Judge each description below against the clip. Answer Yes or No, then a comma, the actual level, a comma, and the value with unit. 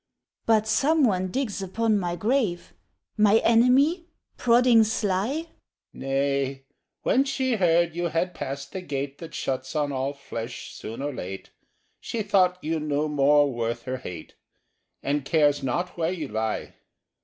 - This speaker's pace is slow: No, average, 145 wpm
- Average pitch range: No, wide, 7.8 semitones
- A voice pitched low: No, medium, 170 Hz